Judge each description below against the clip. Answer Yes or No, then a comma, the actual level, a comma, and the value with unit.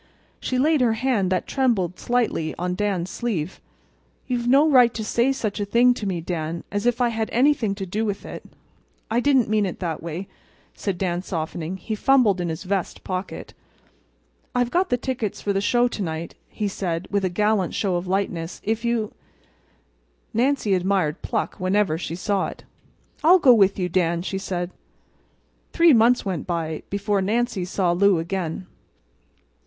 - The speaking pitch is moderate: No, high, 200 Hz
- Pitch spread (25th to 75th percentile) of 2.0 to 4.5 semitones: No, average, 4.9 semitones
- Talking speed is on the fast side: No, average, 175 wpm